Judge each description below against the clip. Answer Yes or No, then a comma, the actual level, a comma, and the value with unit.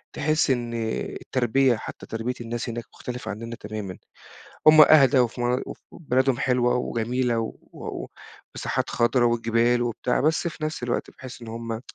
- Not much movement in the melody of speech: Yes, narrow, 1.9 semitones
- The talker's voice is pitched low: Yes, low, 120 Hz